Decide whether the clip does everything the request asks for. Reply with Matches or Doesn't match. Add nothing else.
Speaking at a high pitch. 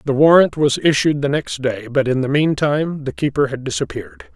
Doesn't match